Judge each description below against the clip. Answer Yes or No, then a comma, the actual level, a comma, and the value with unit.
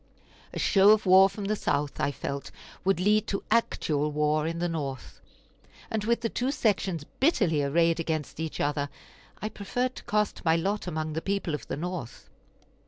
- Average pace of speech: Yes, average, 180 wpm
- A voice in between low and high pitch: Yes, medium, 175 Hz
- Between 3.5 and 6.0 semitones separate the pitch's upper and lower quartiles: Yes, wide, 5.4 semitones